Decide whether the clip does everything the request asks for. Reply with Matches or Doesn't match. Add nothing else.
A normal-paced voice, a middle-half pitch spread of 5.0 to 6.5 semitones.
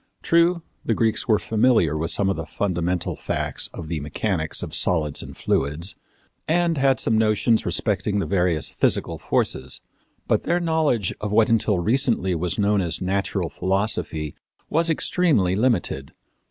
Matches